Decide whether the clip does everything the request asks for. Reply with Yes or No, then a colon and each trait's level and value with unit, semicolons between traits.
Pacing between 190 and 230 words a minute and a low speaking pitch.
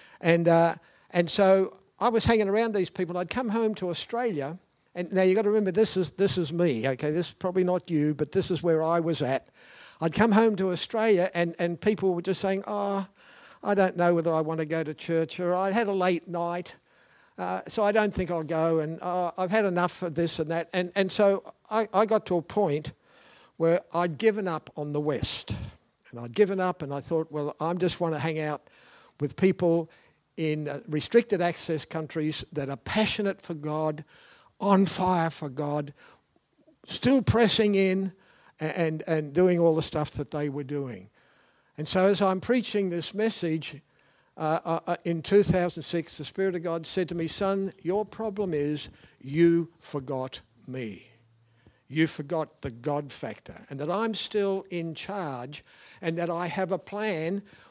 No: average, 195 wpm; medium, 175 Hz